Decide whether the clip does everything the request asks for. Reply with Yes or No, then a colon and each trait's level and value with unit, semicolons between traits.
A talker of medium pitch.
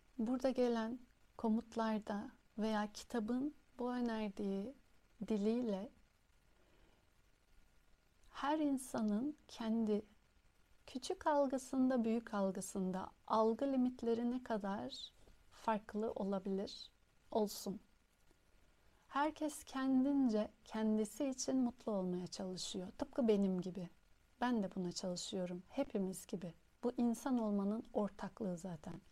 No: high, 220 Hz